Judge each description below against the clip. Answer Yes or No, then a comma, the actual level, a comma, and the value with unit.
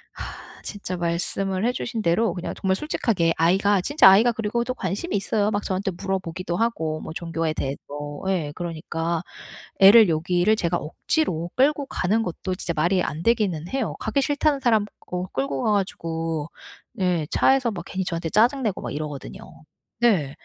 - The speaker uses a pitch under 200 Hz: Yes, medium, 185 Hz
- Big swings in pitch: No, average, 4.9 semitones